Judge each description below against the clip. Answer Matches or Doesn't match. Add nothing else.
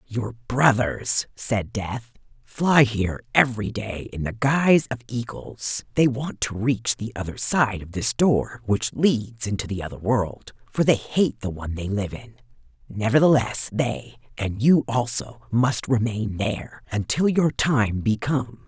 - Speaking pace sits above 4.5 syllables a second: Doesn't match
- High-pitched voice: Doesn't match